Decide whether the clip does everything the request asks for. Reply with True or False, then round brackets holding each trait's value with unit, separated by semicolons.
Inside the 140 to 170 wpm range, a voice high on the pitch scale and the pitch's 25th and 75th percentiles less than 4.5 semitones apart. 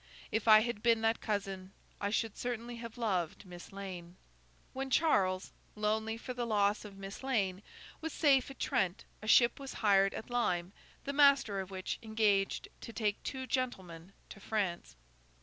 True (165 wpm; 215 Hz; 3.6 semitones)